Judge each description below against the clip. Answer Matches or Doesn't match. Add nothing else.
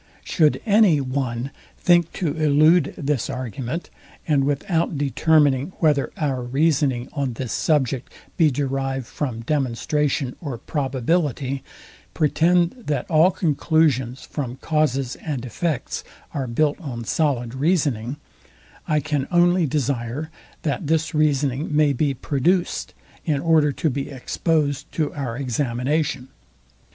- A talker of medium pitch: Matches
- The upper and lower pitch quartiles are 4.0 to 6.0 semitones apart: Doesn't match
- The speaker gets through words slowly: Matches